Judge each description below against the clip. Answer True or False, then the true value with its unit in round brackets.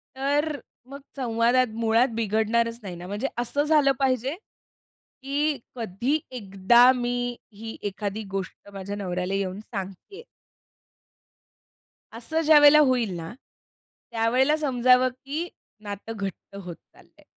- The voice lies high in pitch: True (240 Hz)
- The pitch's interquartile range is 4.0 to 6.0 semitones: True (5.1 semitones)